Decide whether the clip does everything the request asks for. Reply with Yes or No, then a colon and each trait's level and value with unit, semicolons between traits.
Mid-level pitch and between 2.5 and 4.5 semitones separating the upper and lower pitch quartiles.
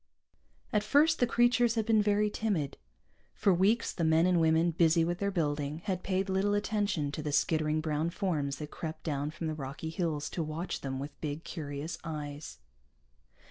No: medium, 165 Hz; average, 4.9 semitones